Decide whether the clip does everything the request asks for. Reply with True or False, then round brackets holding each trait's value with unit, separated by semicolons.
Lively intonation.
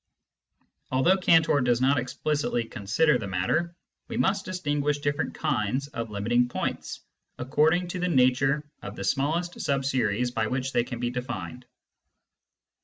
False (4.2 semitones)